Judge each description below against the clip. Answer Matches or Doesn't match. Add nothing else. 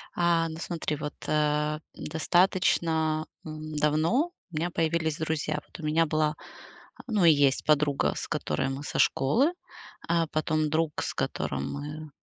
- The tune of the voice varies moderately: Doesn't match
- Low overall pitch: Doesn't match